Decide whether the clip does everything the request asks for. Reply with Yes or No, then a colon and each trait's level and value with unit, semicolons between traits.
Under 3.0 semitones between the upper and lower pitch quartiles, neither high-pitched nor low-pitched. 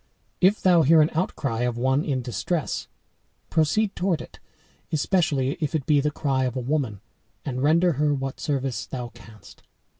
No: average, 3.8 semitones; medium, 145 Hz